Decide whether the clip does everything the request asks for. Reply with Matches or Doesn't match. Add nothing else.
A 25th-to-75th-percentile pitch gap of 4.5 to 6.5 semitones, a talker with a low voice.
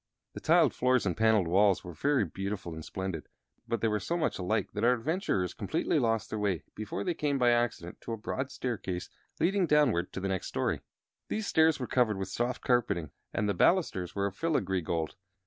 Matches